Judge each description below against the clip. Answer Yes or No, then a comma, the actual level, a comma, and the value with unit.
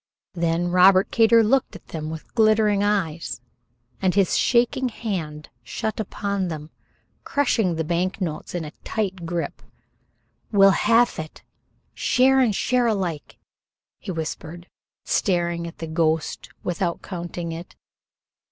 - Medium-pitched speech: Yes, medium, 180 Hz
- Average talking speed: No, slow, 130 wpm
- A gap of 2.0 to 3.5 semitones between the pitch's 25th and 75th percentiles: No, average, 4.5 semitones